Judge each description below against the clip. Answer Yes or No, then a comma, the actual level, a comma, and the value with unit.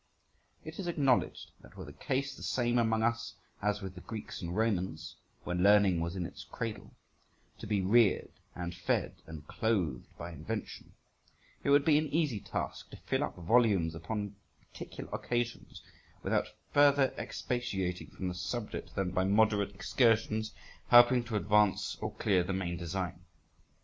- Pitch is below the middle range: Yes, low, 105 Hz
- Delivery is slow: No, average, 160 wpm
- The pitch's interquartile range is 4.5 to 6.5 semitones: Yes, average, 4.8 semitones